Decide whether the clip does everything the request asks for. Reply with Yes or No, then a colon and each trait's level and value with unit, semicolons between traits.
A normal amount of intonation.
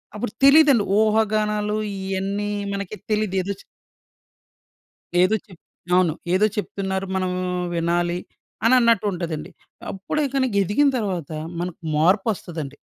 Yes: average, 3.0 semitones